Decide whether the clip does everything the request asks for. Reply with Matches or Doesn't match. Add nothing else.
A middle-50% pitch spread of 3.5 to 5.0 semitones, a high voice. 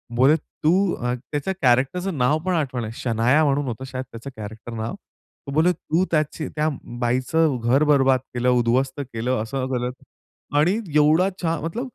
Doesn't match